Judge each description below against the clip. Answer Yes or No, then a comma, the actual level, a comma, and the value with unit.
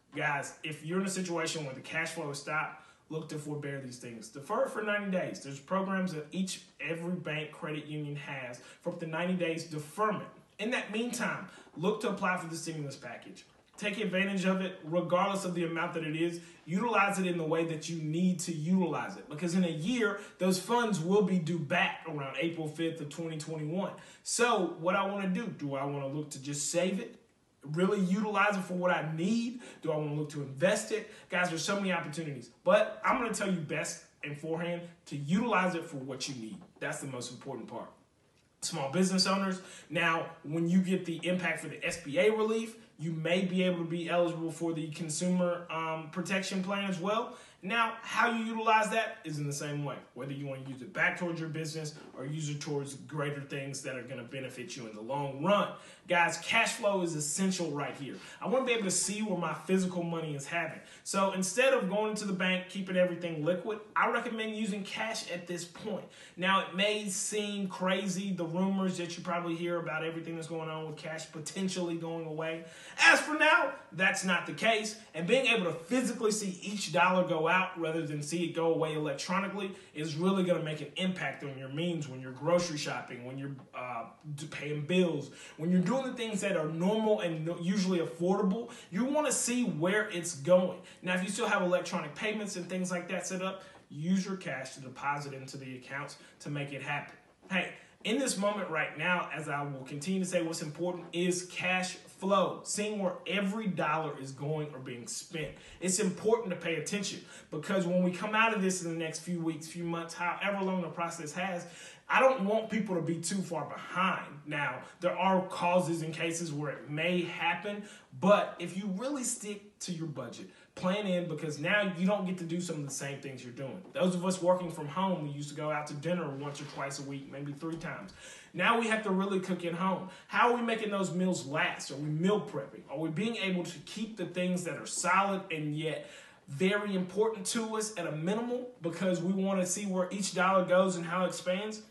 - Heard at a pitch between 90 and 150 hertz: No, medium, 175 Hz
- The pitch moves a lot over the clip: No, average, 3.4 semitones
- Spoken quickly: Yes, fast, 215 wpm